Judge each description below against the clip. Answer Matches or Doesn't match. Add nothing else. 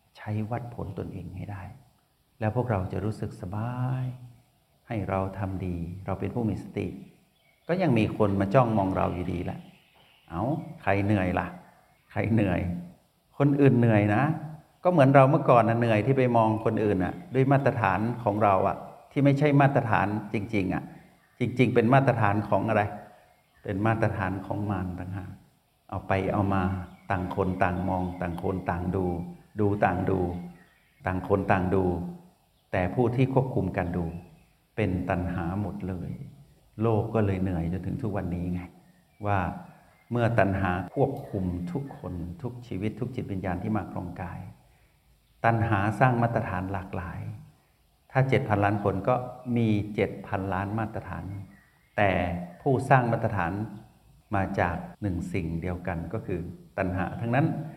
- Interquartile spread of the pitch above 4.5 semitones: Doesn't match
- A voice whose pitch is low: Matches